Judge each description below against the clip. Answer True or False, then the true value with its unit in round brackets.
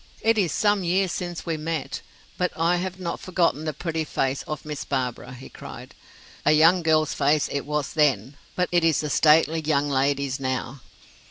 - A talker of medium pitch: True (155 Hz)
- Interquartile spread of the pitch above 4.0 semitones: False (3.6 semitones)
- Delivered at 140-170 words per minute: False (185 wpm)